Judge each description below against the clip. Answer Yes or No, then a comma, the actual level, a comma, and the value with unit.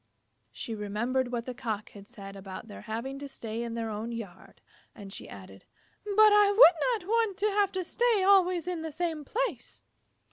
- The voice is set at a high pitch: Yes, very high, 265 Hz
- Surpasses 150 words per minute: Yes, average, 190 wpm